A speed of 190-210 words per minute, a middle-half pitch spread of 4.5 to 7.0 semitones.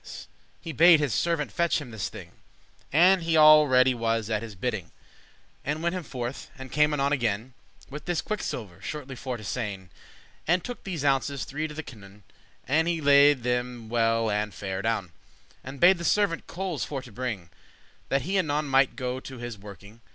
Yes: average, 195 wpm; average, 5.2 semitones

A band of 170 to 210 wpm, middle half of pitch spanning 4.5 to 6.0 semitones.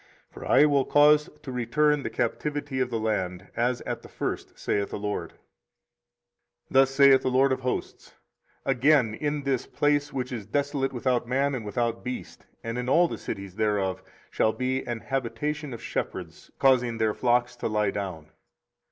No: average, 175 wpm; average, 3.7 semitones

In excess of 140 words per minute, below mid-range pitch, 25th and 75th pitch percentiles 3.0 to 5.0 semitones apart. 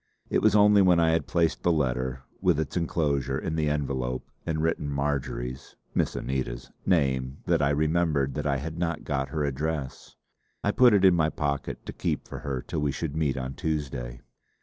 Yes: average, 195 wpm; very low, 75 Hz; average, 3.4 semitones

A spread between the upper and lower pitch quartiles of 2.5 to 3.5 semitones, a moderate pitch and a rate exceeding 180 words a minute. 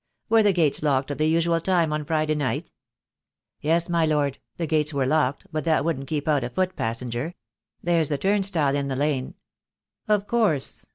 Yes: average, 3.2 semitones; medium, 155 Hz; average, 190 wpm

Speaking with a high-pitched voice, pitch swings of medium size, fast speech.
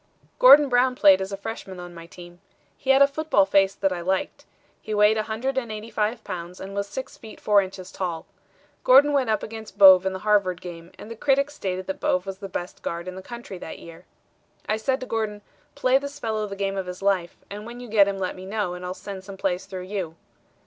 Yes: high, 200 Hz; average, 3.4 semitones; fast, 230 wpm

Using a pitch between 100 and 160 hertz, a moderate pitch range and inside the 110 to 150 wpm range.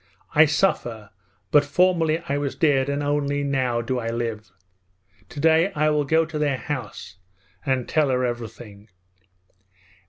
Yes: medium, 140 Hz; average, 4.2 semitones; average, 145 wpm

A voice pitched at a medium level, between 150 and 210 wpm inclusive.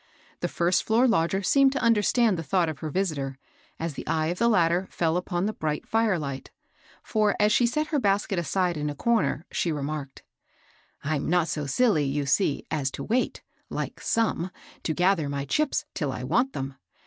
Yes: medium, 175 Hz; fast, 205 wpm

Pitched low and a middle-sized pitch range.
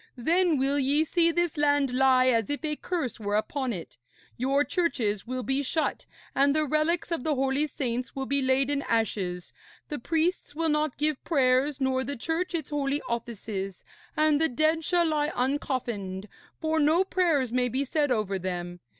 No: very high, 275 Hz; average, 3.9 semitones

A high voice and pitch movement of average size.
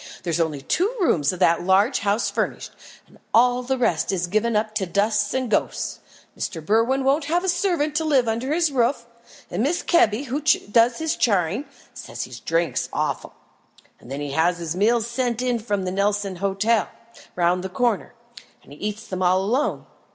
No: high, 215 Hz; wide, 5.7 semitones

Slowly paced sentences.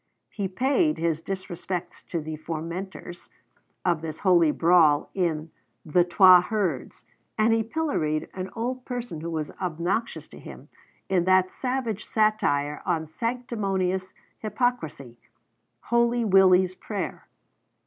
Yes: slow, 120 wpm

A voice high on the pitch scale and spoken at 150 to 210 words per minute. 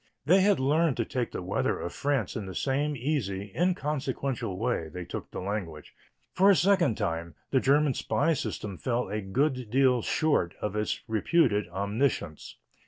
No: low, 125 Hz; average, 170 wpm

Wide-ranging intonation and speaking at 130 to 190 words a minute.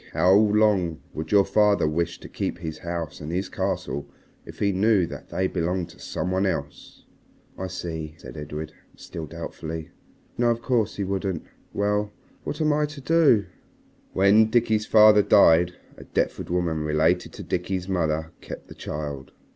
No: average, 4.5 semitones; average, 165 wpm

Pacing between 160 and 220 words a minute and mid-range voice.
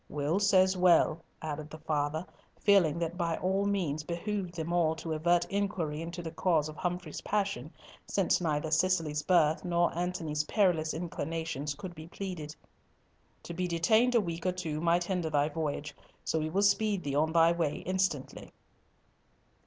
Yes: average, 170 wpm; medium, 170 Hz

